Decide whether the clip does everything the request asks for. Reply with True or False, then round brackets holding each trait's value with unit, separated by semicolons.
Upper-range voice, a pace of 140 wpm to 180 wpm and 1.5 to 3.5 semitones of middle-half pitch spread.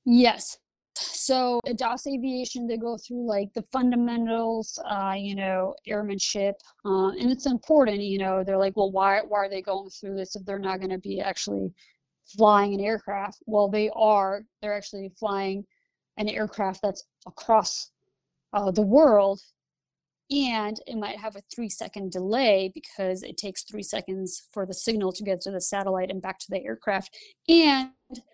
True (205 Hz; 170 wpm; 3.0 semitones)